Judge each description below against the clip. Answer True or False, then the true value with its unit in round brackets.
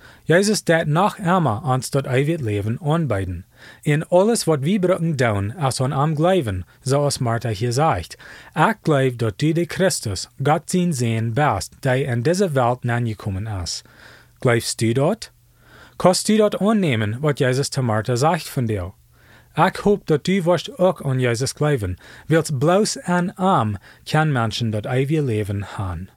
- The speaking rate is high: False (165 wpm)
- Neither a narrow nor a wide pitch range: False (6.5 semitones)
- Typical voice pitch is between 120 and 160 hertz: True (135 Hz)